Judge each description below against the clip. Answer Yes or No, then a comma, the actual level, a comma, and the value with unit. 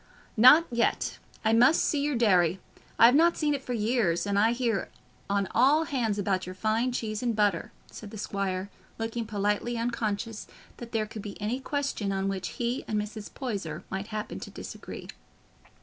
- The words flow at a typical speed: Yes, average, 180 wpm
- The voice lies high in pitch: Yes, high, 220 Hz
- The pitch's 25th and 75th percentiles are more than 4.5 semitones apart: No, average, 3.3 semitones